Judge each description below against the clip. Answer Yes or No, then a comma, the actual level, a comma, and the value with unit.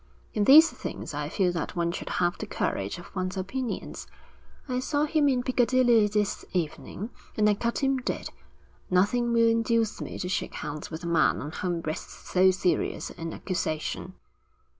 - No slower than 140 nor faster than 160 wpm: No, average, 175 wpm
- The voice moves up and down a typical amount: No, wide, 5.7 semitones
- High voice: Yes, high, 205 Hz